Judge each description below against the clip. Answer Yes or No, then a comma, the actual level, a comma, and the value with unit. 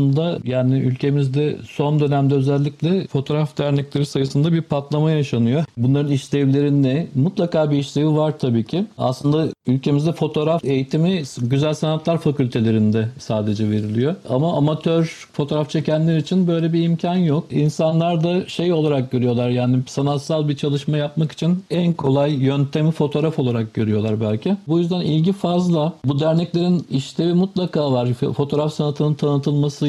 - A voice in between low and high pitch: Yes, medium, 150 Hz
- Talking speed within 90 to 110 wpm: No, fast, 140 wpm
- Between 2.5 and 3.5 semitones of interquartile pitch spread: Yes, average, 2.9 semitones